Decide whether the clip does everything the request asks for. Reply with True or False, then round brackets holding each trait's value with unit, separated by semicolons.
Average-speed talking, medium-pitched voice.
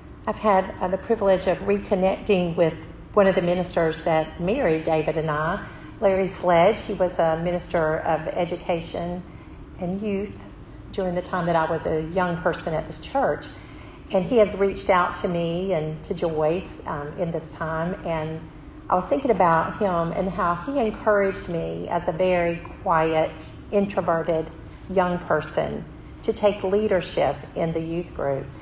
True (160 wpm; 175 Hz)